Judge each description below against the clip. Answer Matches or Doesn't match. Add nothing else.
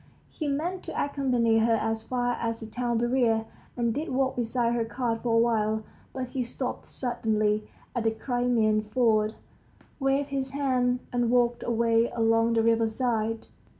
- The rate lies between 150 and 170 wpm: Matches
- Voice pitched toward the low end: Doesn't match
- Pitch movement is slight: Matches